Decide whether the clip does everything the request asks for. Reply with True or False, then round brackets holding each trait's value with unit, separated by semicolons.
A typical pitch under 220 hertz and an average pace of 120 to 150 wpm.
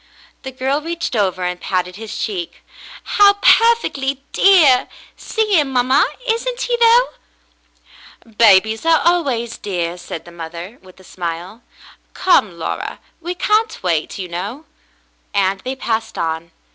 False (230 Hz; 140 wpm)